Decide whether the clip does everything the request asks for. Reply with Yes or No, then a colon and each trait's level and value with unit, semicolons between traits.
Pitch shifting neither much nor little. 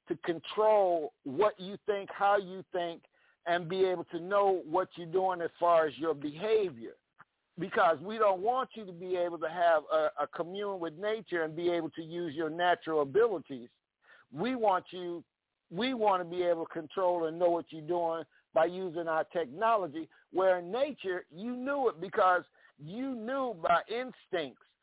Yes: average, 3.8 semitones